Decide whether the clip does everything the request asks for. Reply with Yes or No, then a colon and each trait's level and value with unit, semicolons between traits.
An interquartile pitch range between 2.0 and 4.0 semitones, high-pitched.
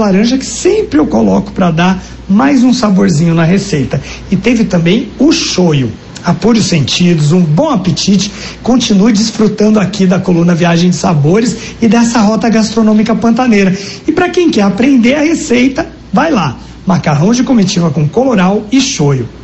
No: average, 5.2 semitones; high, 205 Hz